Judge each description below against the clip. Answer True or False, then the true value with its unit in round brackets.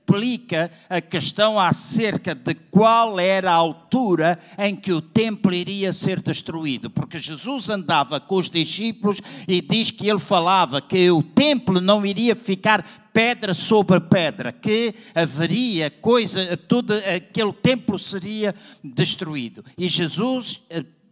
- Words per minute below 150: True (130 wpm)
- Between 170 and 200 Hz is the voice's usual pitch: True (190 Hz)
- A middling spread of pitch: True (4.2 semitones)